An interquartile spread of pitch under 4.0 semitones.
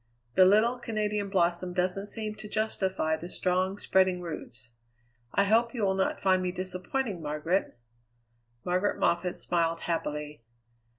Yes: average, 3.1 semitones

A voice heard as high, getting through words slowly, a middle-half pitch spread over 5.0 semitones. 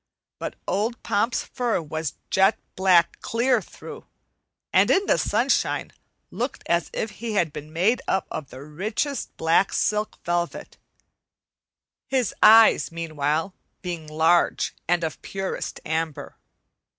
No: medium, 175 Hz; slow, 130 wpm; wide, 5.4 semitones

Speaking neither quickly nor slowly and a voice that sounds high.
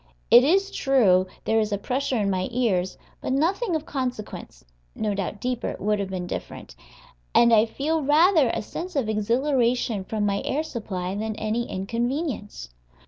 Yes: average, 170 wpm; high, 230 Hz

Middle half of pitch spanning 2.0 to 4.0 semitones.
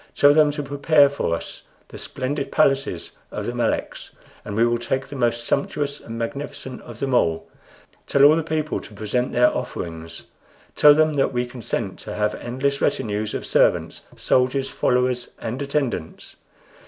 Yes: average, 3.4 semitones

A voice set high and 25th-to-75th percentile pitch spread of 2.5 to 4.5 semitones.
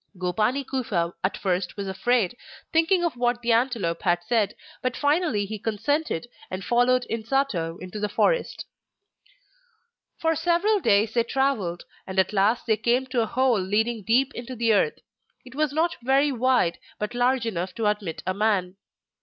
No: high, 230 Hz; average, 4.9 semitones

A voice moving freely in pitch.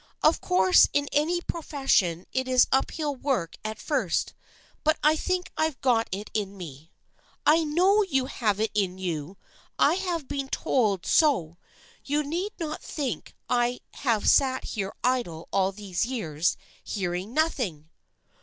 Yes: wide, 7.9 semitones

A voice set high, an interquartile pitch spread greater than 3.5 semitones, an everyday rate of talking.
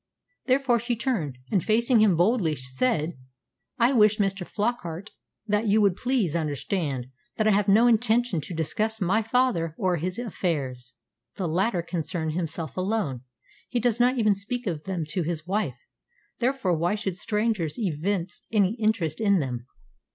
Yes: high, 195 Hz; average, 5.2 semitones; average, 160 wpm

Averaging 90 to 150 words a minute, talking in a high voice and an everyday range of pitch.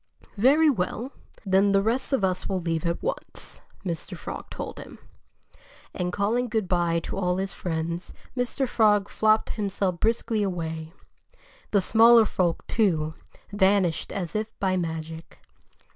Yes: average, 145 wpm; high, 195 Hz; average, 4.1 semitones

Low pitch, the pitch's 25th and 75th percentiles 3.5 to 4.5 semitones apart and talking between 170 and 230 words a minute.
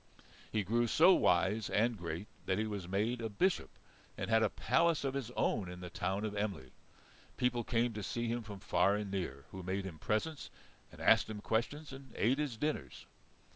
Yes: low, 110 Hz; average, 4.0 semitones; average, 200 wpm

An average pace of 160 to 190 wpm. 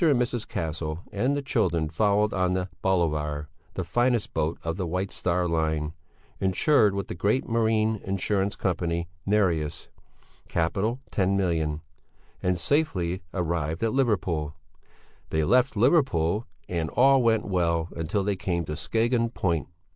No: average, 140 wpm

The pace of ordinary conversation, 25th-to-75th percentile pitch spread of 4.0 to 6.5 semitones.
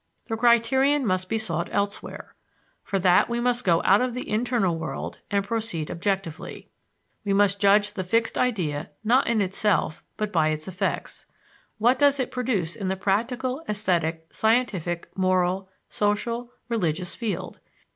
Yes: average, 150 wpm; average, 4.4 semitones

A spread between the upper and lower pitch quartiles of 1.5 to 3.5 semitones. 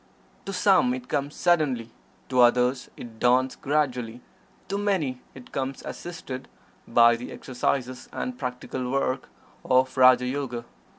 Yes: narrow, 2.4 semitones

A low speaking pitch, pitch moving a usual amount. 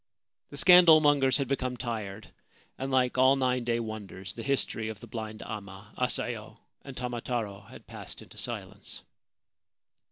Yes: low, 120 Hz; average, 3.3 semitones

